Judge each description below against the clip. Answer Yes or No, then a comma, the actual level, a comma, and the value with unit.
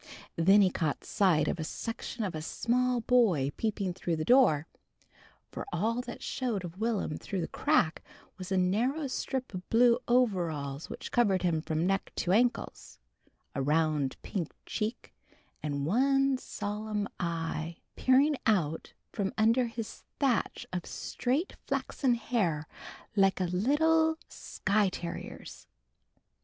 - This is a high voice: Yes, high, 200 Hz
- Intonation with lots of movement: Yes, wide, 6.4 semitones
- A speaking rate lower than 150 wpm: Yes, average, 140 wpm